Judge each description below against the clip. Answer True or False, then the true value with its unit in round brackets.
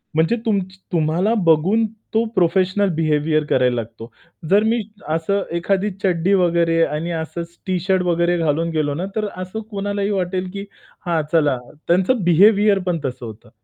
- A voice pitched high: False (175 Hz)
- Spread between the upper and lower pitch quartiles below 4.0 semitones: True (3.6 semitones)